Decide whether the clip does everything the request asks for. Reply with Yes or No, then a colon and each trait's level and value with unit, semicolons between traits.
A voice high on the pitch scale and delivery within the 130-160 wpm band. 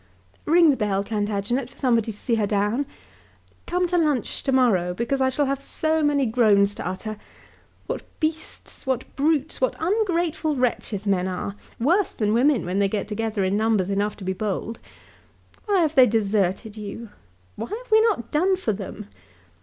No: high, 235 Hz; average, 175 wpm